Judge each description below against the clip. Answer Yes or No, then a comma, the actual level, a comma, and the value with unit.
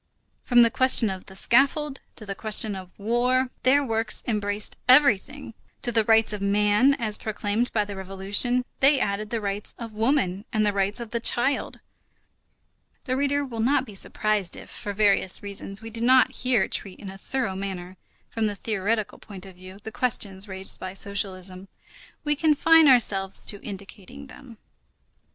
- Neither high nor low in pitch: No, high, 215 Hz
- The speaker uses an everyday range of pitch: Yes, average, 4.1 semitones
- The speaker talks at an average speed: Yes, average, 175 wpm